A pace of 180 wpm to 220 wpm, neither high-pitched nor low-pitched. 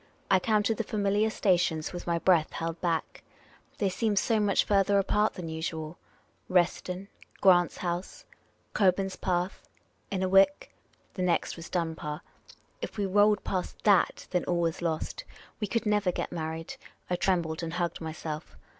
No: average, 160 wpm; medium, 180 Hz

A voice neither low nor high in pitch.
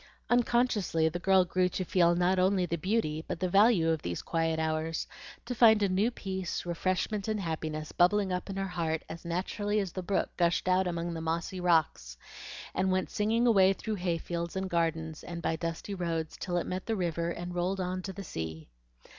Yes: medium, 180 Hz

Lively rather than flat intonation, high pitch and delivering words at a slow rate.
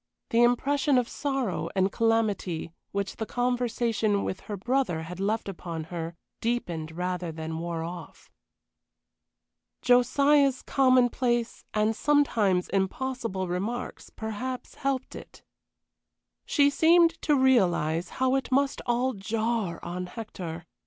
Yes: wide, 6.1 semitones; high, 225 Hz; slow, 120 wpm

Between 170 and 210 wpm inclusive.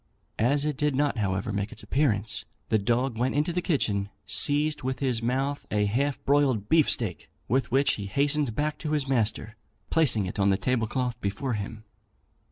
Yes: average, 180 wpm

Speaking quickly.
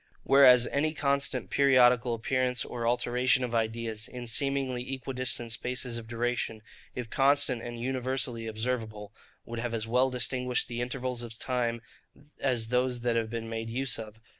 No: average, 155 wpm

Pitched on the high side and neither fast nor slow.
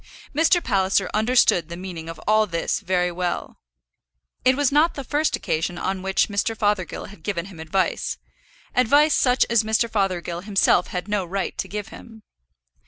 Yes: high, 200 Hz; average, 170 wpm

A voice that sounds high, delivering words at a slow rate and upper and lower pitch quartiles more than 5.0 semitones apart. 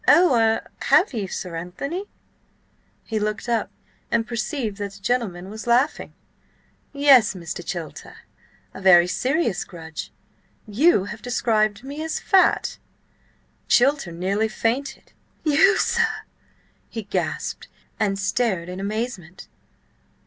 Yes: high, 220 Hz; slow, 115 wpm; wide, 5.4 semitones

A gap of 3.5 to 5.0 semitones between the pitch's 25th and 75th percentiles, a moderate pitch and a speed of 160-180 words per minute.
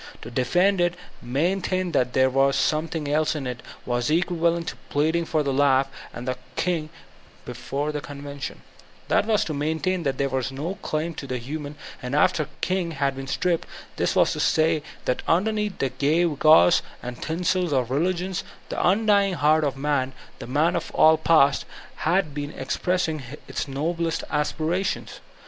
Yes: average, 3.9 semitones; medium, 155 Hz; average, 175 wpm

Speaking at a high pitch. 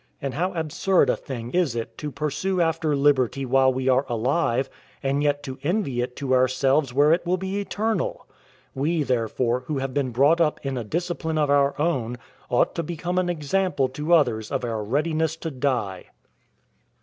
No: medium, 145 Hz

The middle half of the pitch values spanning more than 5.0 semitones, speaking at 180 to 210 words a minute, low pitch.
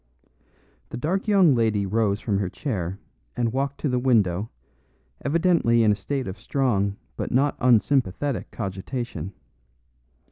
No: wide, 5.5 semitones; slow, 135 wpm; low, 115 Hz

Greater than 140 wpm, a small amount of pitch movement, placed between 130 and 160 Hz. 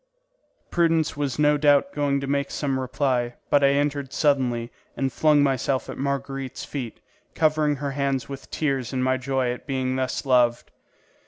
Yes: average, 165 wpm; narrow, 1.8 semitones; medium, 140 Hz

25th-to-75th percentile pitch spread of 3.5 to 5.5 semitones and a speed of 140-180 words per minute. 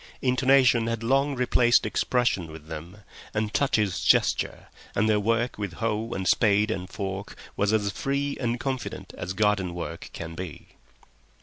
Yes: average, 4.2 semitones; average, 150 wpm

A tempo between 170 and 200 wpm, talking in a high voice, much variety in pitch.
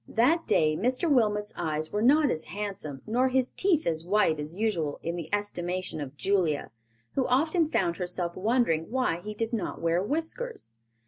Yes: average, 175 wpm; high, 205 Hz; wide, 7.3 semitones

